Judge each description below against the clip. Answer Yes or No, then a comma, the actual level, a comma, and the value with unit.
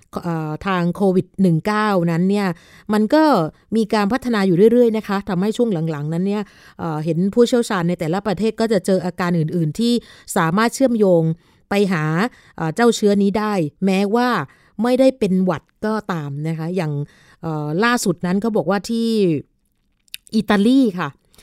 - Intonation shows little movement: No, average, 4.5 semitones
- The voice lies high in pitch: Yes, high, 195 Hz